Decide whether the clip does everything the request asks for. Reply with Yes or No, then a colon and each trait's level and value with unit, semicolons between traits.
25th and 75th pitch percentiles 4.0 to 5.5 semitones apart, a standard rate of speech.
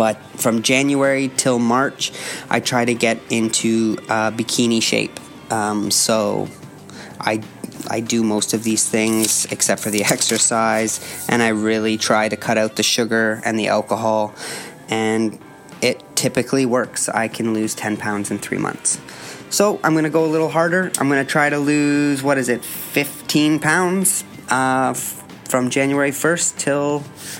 Yes: average, 4.4 semitones; average, 160 wpm